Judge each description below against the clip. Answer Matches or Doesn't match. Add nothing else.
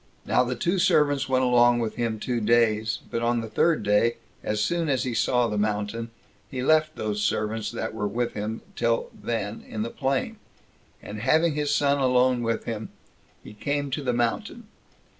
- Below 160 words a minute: Doesn't match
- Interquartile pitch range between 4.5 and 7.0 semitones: Doesn't match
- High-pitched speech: Doesn't match